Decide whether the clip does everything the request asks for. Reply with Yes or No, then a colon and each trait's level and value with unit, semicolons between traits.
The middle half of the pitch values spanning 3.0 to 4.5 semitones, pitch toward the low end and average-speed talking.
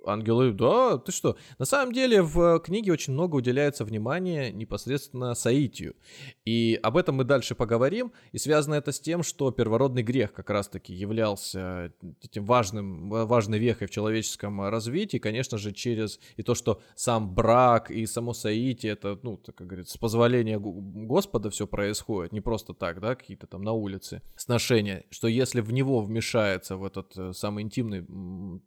No: average, 3.9 semitones; low, 115 Hz; fast, 165 wpm